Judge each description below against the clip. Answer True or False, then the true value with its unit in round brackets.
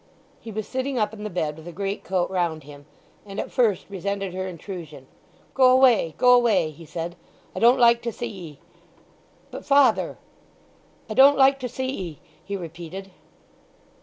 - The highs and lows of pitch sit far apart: True (5.9 semitones)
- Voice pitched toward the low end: False (200 Hz)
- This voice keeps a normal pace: True (165 wpm)